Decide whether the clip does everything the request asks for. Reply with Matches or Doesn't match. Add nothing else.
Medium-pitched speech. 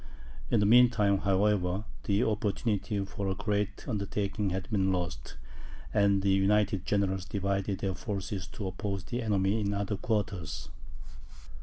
Doesn't match